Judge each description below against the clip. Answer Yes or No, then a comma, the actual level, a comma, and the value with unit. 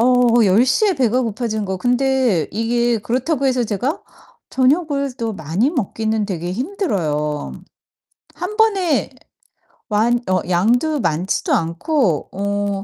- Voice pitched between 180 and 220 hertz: No, high, 235 Hz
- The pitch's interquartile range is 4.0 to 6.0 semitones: Yes, average, 5.1 semitones